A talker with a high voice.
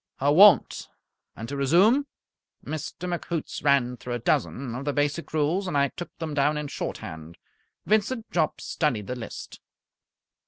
No: medium, 145 Hz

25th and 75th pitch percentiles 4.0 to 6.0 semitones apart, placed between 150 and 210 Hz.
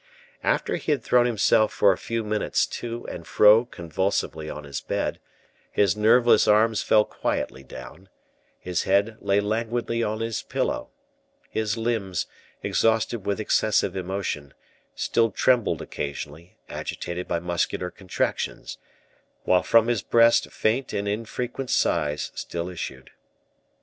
No: average, 4.3 semitones; low, 105 Hz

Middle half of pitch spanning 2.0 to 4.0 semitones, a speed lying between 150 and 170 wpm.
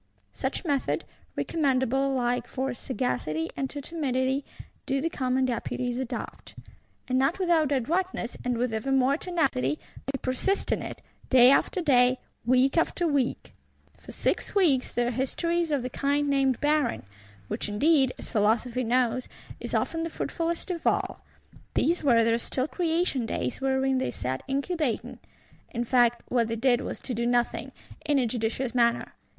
Yes: average, 3.3 semitones; average, 160 wpm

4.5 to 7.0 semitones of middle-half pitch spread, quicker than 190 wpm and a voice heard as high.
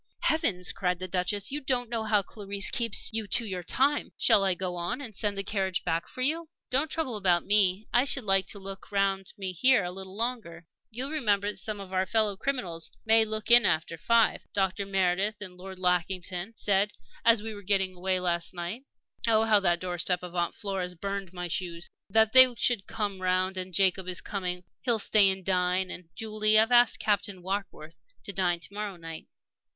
No: average, 3.2 semitones; average, 200 wpm; high, 195 Hz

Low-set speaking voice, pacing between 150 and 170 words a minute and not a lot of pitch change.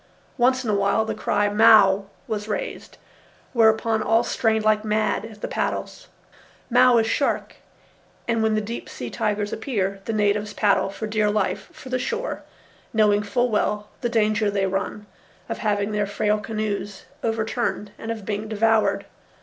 No: high, 215 Hz; average, 165 wpm; narrow, 1.4 semitones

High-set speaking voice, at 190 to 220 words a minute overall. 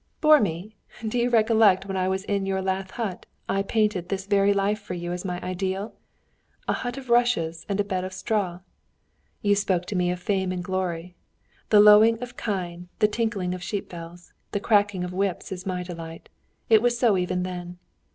Yes: high, 195 Hz; average, 200 wpm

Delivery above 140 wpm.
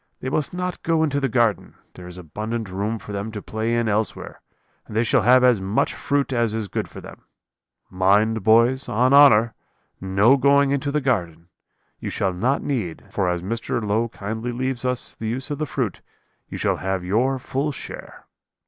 Yes: average, 195 wpm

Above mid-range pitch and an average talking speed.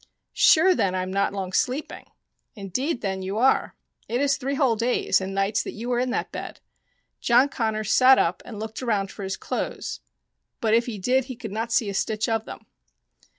No: high, 225 Hz; fast, 220 wpm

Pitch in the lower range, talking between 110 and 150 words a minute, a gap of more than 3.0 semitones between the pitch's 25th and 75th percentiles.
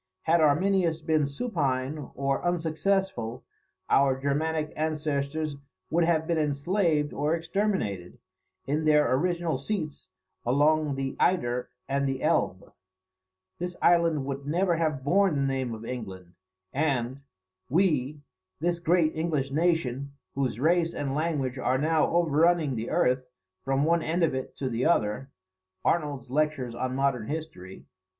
No: medium, 150 Hz; slow, 135 wpm; average, 3.6 semitones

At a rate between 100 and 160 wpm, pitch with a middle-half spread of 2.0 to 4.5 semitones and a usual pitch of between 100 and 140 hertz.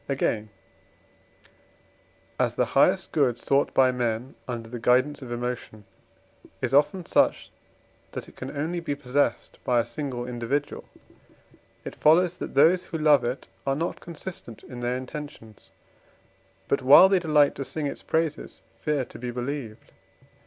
Yes: average, 150 wpm; average, 3.7 semitones; low, 135 Hz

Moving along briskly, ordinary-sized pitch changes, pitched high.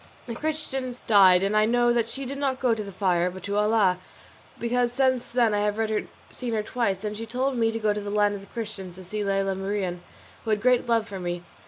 Yes: fast, 240 wpm; average, 3.5 semitones; high, 215 Hz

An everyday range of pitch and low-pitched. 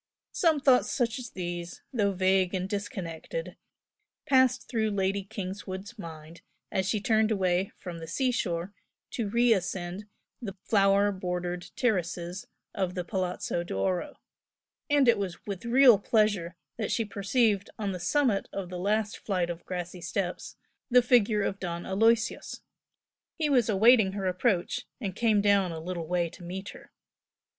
No: average, 3.9 semitones; high, 195 Hz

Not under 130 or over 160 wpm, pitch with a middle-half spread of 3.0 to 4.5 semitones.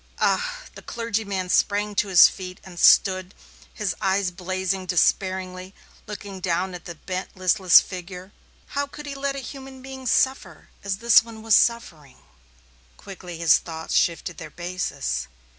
Yes: average, 150 wpm; average, 3.7 semitones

